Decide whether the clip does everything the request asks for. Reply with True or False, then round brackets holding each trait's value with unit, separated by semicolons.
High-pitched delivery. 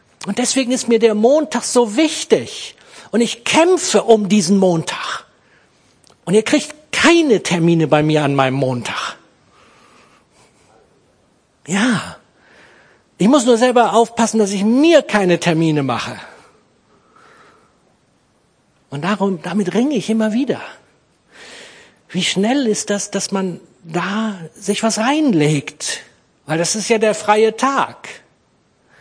True (210 Hz)